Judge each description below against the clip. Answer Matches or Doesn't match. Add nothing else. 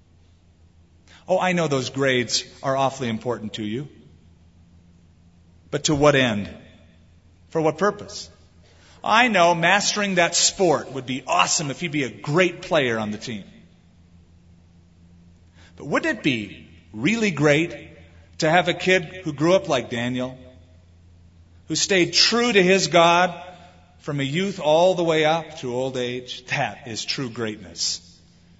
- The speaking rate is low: Doesn't match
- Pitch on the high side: Doesn't match